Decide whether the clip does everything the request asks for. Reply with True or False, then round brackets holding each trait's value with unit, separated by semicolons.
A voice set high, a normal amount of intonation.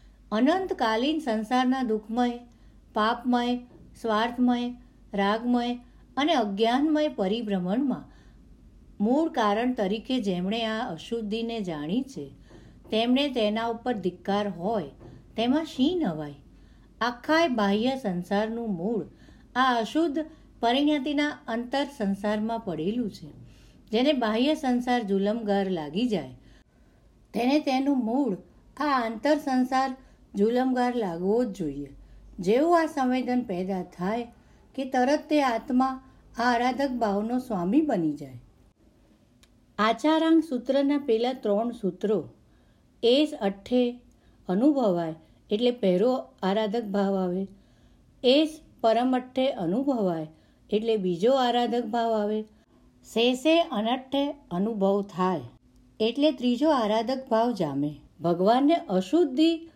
True (230 Hz; 4.4 semitones)